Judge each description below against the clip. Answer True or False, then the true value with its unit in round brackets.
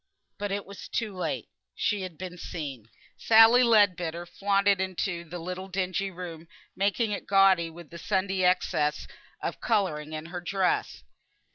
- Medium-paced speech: True (150 wpm)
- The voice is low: False (185 Hz)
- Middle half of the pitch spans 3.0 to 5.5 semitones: False (2.6 semitones)